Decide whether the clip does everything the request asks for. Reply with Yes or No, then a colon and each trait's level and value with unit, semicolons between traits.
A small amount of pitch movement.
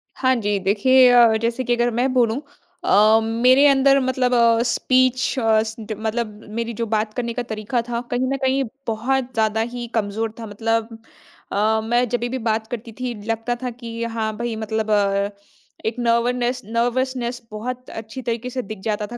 Yes: narrow, 2.1 semitones